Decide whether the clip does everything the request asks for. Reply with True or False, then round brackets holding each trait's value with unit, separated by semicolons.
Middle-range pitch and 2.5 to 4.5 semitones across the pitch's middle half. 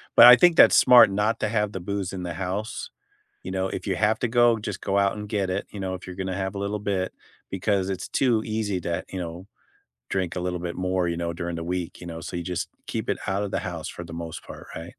False (95 Hz; 2.8 semitones)